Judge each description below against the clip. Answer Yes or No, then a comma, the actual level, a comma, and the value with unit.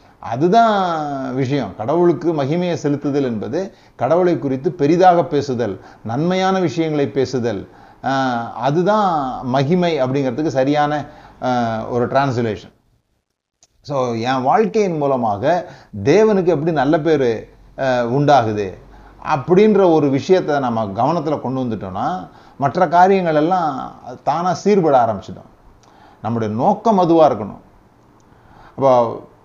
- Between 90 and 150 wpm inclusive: Yes, average, 95 wpm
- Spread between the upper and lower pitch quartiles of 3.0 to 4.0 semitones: No, wide, 5.5 semitones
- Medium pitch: Yes, medium, 145 Hz